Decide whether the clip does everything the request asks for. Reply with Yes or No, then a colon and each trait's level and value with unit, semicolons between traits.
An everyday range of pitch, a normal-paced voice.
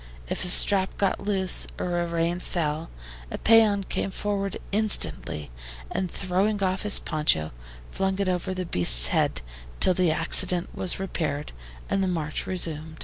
Yes: average, 3.2 semitones; average, 155 wpm